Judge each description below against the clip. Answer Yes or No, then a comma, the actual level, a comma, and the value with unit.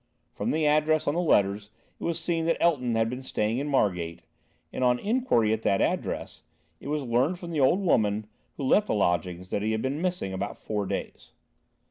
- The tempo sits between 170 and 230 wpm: Yes, fast, 205 wpm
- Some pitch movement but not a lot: No, wide, 7.3 semitones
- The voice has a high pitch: No, low, 125 Hz